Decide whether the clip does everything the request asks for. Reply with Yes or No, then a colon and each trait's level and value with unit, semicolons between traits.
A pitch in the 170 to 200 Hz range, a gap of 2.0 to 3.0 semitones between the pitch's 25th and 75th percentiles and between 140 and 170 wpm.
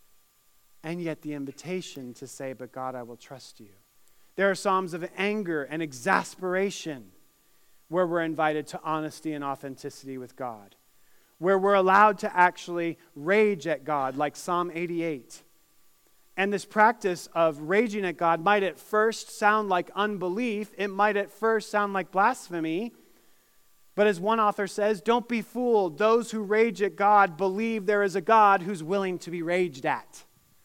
No: medium, 185 Hz; average, 4.9 semitones; average, 165 wpm